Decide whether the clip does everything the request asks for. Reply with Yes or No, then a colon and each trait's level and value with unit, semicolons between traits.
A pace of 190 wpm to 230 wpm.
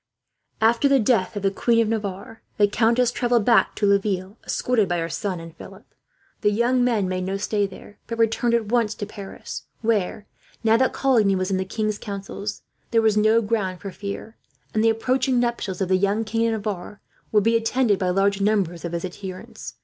Yes: fast, 205 wpm